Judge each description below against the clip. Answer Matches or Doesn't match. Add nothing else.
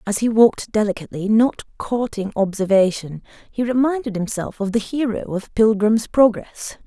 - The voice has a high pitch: Matches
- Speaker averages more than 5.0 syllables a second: Doesn't match